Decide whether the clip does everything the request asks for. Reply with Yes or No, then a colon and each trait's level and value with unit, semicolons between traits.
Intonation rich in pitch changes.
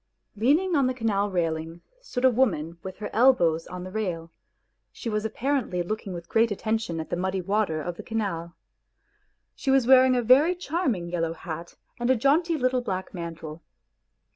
Yes: wide, 6.8 semitones